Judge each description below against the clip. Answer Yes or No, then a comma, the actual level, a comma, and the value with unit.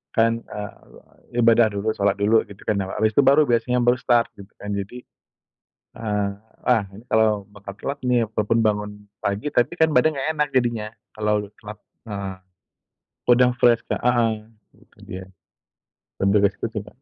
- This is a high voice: No, low, 110 Hz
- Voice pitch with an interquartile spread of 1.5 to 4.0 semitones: Yes, average, 2.9 semitones